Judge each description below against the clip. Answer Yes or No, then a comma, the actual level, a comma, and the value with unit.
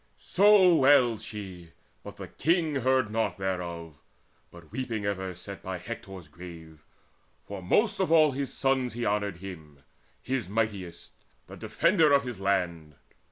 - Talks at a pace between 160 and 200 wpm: No, average, 145 wpm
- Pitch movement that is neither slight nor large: No, wide, 6.8 semitones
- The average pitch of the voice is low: Yes, low, 105 Hz